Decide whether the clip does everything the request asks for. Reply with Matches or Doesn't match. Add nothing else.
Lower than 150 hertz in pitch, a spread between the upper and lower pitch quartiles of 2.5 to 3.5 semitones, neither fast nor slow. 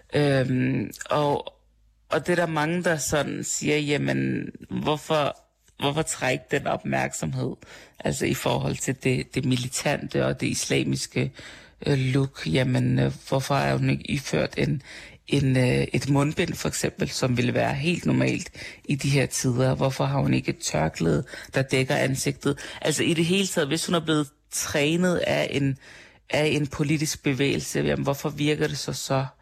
Matches